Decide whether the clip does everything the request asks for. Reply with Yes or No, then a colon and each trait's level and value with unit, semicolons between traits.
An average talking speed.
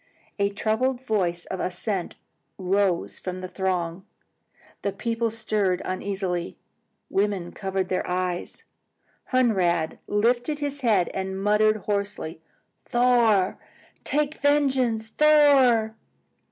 No: slow, 100 wpm